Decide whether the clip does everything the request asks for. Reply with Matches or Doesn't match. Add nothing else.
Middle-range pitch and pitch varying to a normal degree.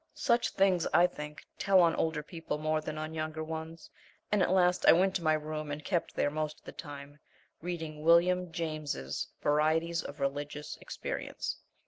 Doesn't match